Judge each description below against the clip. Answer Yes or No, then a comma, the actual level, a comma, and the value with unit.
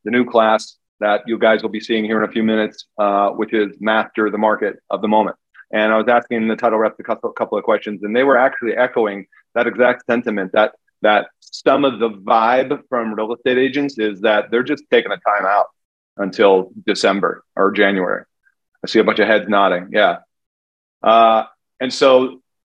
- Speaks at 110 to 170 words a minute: No, fast, 205 wpm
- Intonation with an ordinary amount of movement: No, narrow, 2.1 semitones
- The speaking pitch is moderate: No, low, 110 Hz